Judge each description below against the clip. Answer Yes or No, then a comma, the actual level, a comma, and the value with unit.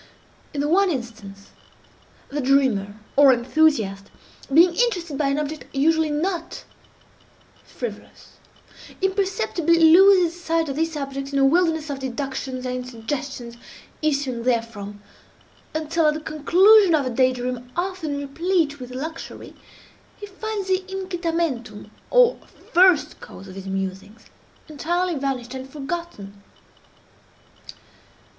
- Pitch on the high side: Yes, very high, 290 Hz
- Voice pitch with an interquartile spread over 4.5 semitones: Yes, average, 5.2 semitones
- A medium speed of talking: No, slow, 120 wpm